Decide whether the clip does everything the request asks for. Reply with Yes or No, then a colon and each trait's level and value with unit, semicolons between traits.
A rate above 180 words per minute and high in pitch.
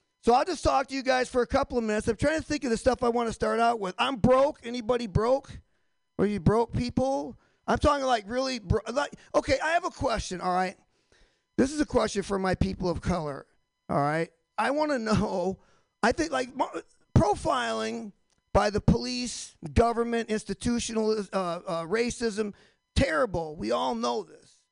Yes: average, 190 wpm; high, 235 Hz